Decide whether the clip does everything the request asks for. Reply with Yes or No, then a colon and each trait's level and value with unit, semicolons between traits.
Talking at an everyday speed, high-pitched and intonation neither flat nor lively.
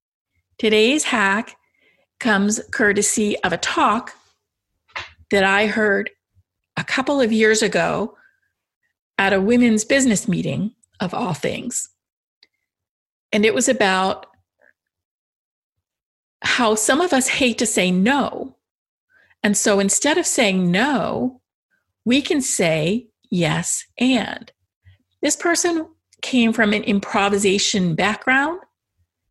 No: slow, 110 wpm; high, 215 Hz; average, 4.7 semitones